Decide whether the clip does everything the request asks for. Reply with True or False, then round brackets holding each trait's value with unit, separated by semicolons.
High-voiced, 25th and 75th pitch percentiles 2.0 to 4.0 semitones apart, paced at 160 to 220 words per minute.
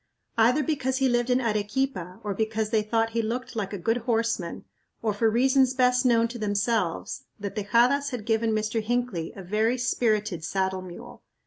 True (225 Hz; 3.0 semitones; 180 wpm)